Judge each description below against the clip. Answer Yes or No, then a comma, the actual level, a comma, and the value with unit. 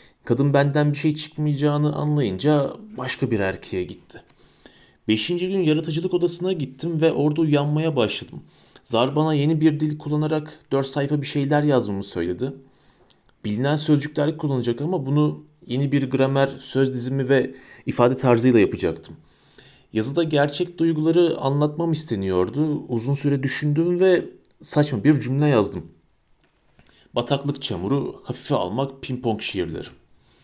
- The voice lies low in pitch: No, medium, 145 Hz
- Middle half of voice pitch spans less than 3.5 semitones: Yes, narrow, 2.5 semitones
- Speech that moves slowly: No, average, 125 wpm